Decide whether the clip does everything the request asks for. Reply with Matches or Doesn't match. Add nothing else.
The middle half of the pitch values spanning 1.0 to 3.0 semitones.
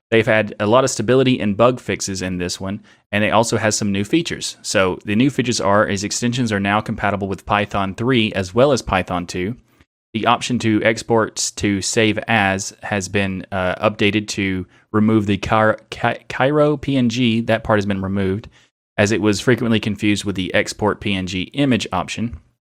Matches